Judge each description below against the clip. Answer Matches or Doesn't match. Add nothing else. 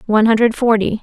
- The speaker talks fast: Doesn't match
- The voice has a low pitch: Doesn't match